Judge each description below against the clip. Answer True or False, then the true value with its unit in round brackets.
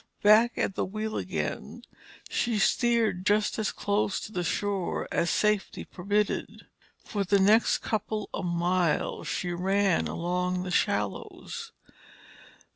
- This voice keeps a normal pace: False (125 wpm)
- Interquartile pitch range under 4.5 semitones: True (2.9 semitones)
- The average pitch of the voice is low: False (200 Hz)